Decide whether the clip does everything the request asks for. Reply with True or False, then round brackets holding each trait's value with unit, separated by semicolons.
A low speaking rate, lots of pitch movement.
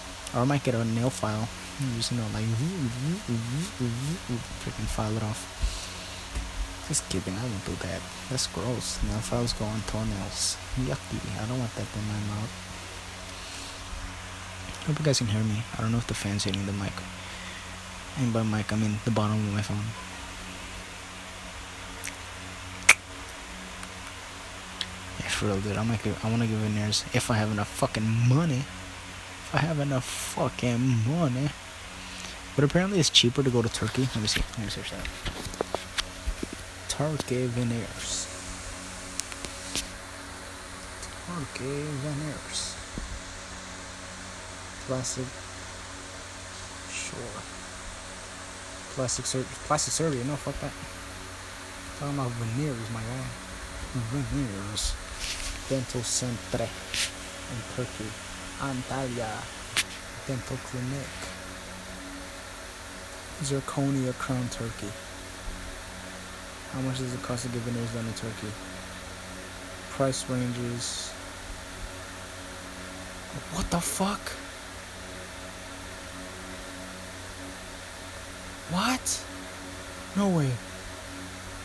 False (115 wpm; 4.3 semitones)